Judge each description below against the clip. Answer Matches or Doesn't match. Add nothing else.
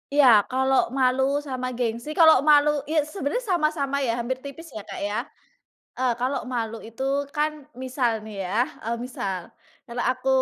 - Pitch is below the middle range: Doesn't match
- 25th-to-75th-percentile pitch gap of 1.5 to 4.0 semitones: Matches